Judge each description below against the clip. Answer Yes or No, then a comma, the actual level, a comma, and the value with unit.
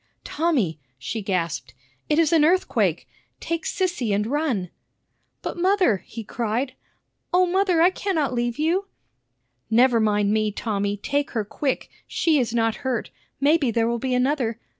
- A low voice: No, very high, 250 Hz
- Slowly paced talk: No, average, 150 wpm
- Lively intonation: Yes, wide, 6.7 semitones